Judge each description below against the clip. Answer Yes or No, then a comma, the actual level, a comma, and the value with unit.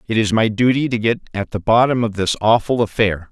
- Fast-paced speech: Yes, fast, 235 wpm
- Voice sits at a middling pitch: No, low, 110 Hz